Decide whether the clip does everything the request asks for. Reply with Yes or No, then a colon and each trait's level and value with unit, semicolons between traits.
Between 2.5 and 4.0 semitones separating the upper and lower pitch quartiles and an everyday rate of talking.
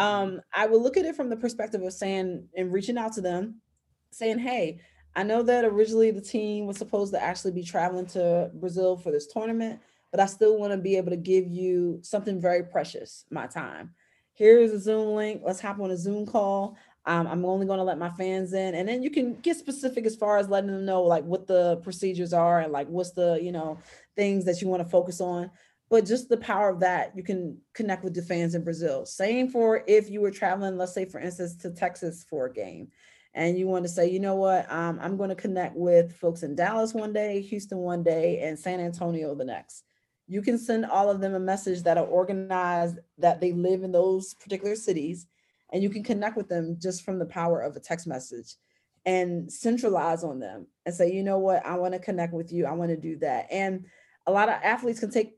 No: average, 3.2 semitones; fast, 235 wpm